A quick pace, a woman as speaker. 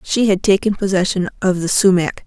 No: average, 185 wpm; female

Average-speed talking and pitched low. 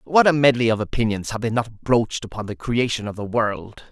No: fast, 230 wpm; low, 115 Hz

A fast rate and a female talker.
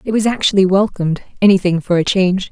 No: average, 190 wpm; female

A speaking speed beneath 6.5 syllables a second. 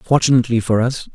No: 6.9 syllables/s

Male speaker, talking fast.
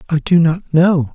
Yes: male; fast, 210 wpm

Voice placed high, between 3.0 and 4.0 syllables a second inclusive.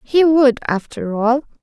Yes: very high, 255 Hz; 3.9 syllables/s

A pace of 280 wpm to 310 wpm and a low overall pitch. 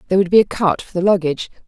No: fast, 285 wpm; medium, 185 Hz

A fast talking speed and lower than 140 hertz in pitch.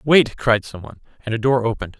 Yes: fast, 210 wpm; low, 115 Hz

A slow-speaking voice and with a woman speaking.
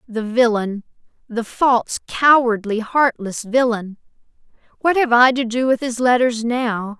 Yes: slow, 120 wpm; female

